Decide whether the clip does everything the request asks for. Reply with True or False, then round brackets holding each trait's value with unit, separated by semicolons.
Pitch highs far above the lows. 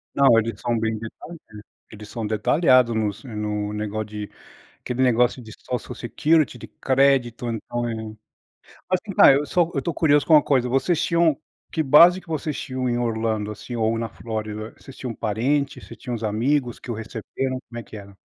False (4.0 semitones)